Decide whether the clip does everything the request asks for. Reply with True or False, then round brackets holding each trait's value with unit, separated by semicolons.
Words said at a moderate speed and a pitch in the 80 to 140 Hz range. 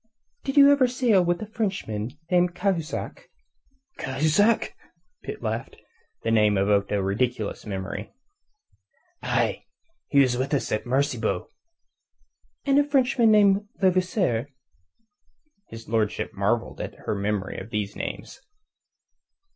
False (120 wpm; 135 Hz)